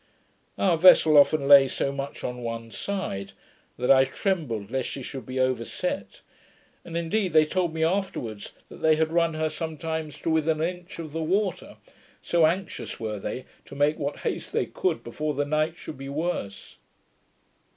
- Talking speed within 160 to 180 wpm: Yes, average, 175 wpm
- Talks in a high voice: No, medium, 155 Hz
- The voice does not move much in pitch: No, average, 3.8 semitones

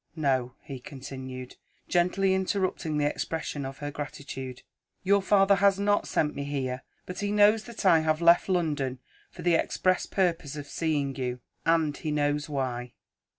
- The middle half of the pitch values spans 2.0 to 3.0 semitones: No, average, 5.2 semitones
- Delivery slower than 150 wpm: No, average, 160 wpm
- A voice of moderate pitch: Yes, medium, 150 Hz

